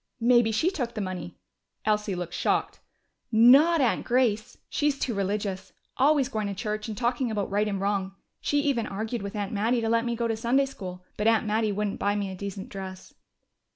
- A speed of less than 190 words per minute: No, average, 200 wpm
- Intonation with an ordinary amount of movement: Yes, average, 3.2 semitones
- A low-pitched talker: No, high, 215 Hz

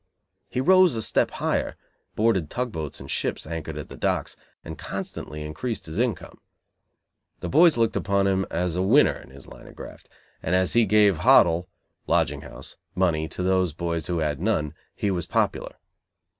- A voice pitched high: No, very low, 90 Hz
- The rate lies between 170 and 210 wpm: Yes, average, 180 wpm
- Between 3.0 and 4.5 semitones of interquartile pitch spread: No, wide, 5.4 semitones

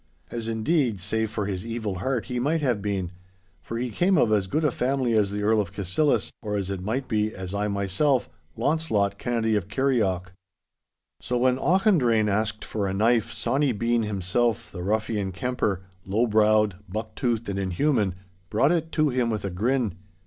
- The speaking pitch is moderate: No, low, 110 Hz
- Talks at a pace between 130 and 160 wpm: No, average, 185 wpm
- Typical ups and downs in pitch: Yes, average, 3.8 semitones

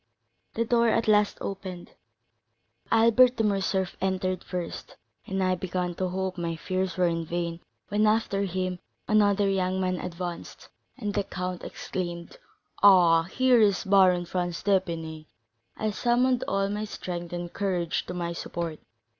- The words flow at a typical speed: Yes, average, 145 wpm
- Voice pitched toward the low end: No, medium, 185 Hz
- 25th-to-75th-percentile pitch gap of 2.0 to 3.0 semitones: Yes, average, 2.7 semitones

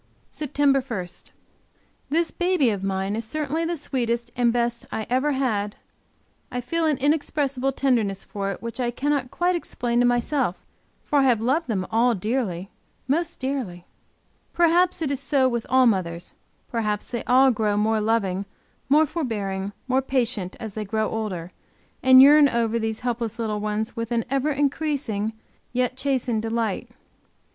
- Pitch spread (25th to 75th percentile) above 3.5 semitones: Yes, average, 4.2 semitones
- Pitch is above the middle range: Yes, high, 240 Hz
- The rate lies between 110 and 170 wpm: Yes, average, 160 wpm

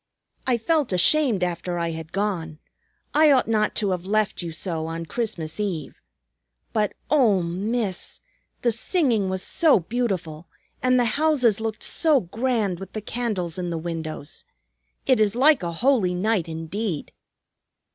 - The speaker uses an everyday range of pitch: No, wide, 5.8 semitones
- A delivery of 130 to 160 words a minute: Yes, average, 150 wpm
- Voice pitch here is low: No, high, 205 Hz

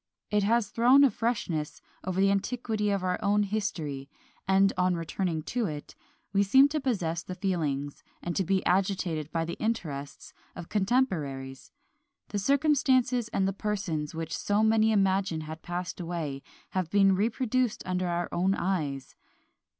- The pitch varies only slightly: No, average, 4.6 semitones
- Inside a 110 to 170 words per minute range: Yes, average, 155 wpm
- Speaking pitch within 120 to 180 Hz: No, high, 190 Hz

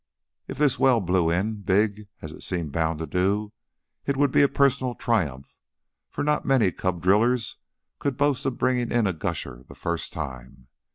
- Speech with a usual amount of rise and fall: No, wide, 7.0 semitones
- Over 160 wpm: Yes, average, 180 wpm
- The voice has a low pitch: Yes, low, 105 Hz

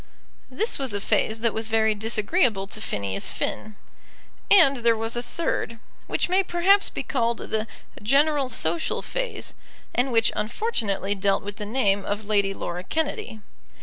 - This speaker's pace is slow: No, average, 155 wpm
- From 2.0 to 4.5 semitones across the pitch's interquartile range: No, average, 5.1 semitones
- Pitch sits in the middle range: No, high, 225 Hz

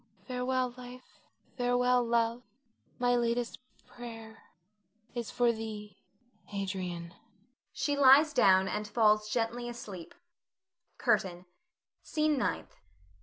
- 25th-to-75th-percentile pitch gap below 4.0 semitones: Yes, average, 2.8 semitones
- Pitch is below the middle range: No, high, 235 Hz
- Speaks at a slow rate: Yes, slow, 95 wpm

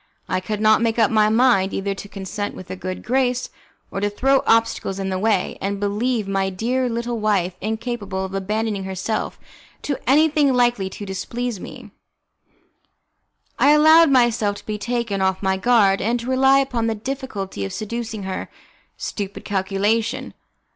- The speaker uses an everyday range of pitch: Yes, average, 3.9 semitones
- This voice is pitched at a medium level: No, high, 215 Hz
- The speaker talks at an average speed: Yes, average, 165 wpm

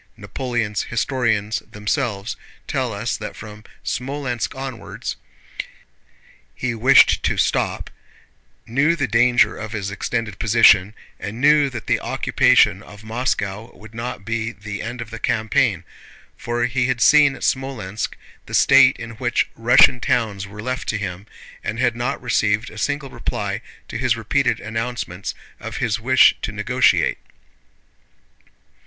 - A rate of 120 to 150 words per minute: Yes, average, 140 wpm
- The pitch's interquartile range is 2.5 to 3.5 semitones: Yes, average, 3.0 semitones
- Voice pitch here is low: Yes, low, 115 Hz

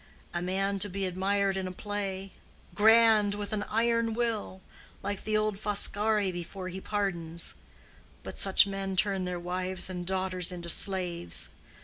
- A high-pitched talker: Yes, high, 195 Hz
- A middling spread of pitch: No, narrow, 2.0 semitones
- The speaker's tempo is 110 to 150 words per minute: Yes, average, 145 wpm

